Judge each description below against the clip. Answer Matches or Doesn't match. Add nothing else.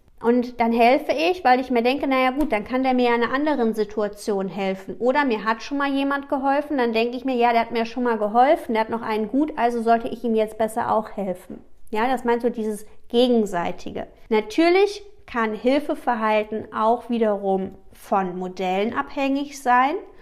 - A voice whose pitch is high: Matches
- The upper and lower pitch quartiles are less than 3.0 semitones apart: Doesn't match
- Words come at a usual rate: Doesn't match